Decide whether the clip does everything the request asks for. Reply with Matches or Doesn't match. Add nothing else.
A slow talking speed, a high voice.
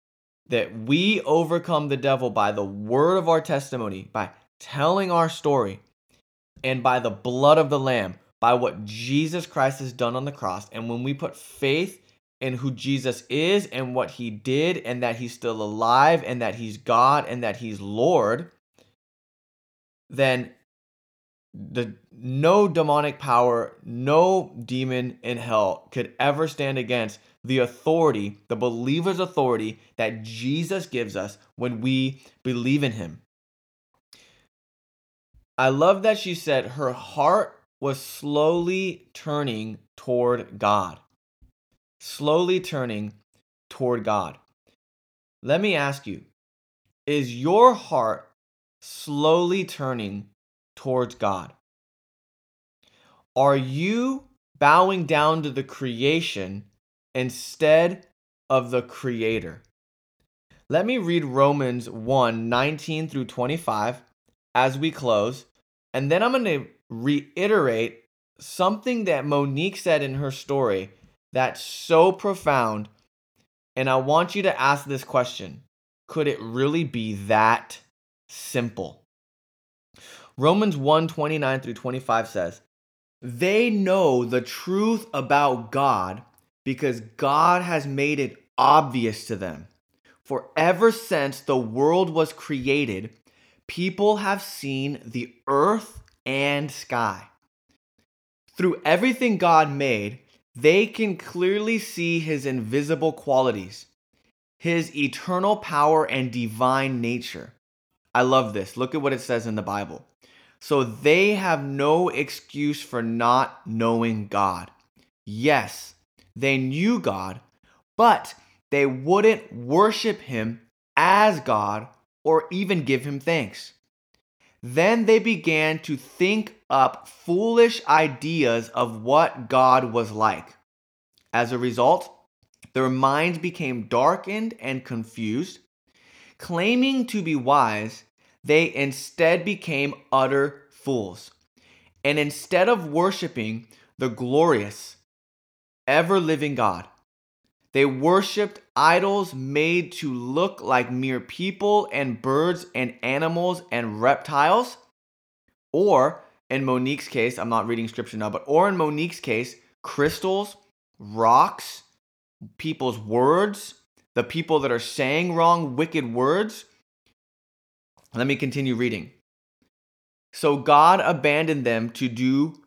Doesn't match